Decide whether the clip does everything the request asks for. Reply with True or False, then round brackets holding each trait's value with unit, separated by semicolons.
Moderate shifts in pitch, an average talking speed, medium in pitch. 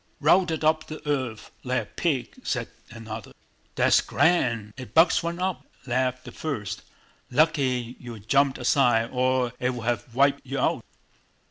False (4.2 semitones; 150 wpm; 130 Hz)